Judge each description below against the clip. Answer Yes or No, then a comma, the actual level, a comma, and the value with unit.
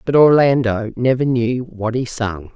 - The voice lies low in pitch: Yes, low, 120 Hz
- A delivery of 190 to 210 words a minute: No, average, 165 wpm